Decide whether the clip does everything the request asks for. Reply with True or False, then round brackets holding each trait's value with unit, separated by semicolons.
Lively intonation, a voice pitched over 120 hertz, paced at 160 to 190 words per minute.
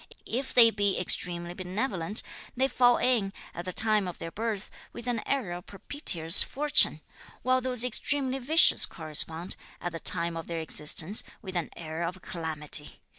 True (6.4 semitones; 190 Hz; 165 wpm)